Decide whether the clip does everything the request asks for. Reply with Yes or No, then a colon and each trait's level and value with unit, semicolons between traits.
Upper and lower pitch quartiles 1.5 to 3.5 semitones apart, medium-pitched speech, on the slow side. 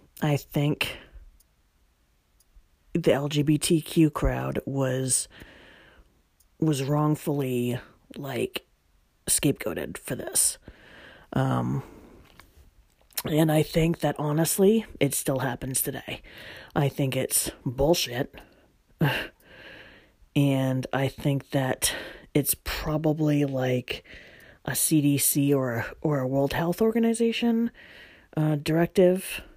Yes: average, 3.1 semitones; medium, 145 Hz; slow, 85 wpm